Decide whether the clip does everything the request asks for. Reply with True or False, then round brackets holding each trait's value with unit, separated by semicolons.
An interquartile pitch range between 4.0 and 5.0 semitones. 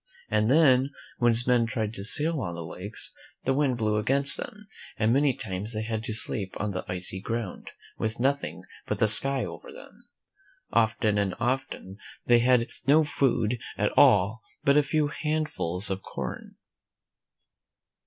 True (4.5 semitones)